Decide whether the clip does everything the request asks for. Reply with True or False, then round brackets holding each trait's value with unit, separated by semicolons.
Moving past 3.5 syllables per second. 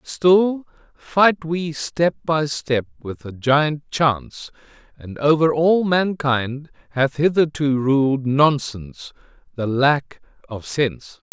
False (3.3 syllables/s)